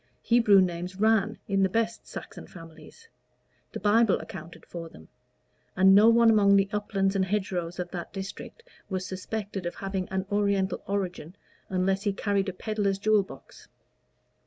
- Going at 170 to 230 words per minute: No, average, 160 wpm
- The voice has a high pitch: Yes, high, 195 Hz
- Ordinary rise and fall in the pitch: No, narrow, 2.0 semitones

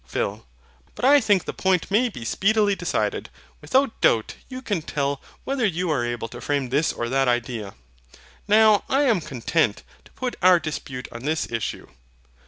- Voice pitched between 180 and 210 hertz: No, medium, 165 Hz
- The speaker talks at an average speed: Yes, average, 175 wpm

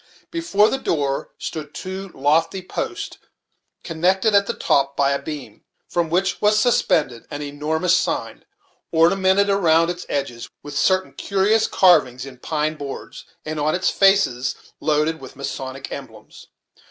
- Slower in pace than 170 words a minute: Yes, average, 140 wpm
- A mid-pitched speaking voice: Yes, medium, 160 Hz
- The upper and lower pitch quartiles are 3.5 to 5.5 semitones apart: Yes, average, 5.2 semitones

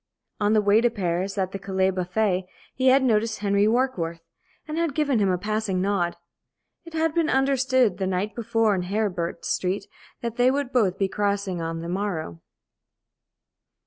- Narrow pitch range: No, average, 4.6 semitones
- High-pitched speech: Yes, high, 205 Hz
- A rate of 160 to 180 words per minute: Yes, average, 175 wpm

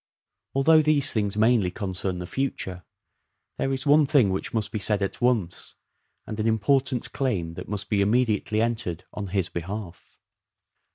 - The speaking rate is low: No, average, 160 wpm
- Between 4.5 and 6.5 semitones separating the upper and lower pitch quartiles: Yes, average, 4.9 semitones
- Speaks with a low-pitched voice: Yes, low, 105 Hz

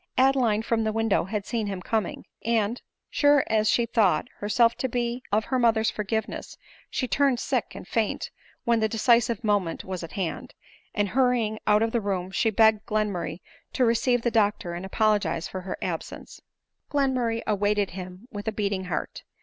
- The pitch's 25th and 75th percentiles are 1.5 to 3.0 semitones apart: Yes, average, 2.7 semitones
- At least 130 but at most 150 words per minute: No, average, 175 wpm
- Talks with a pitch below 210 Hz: No, high, 220 Hz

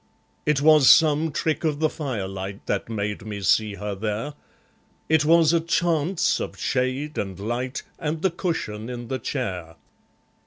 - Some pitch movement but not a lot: No, wide, 6.9 semitones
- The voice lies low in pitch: Yes, low, 130 Hz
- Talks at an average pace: Yes, average, 155 wpm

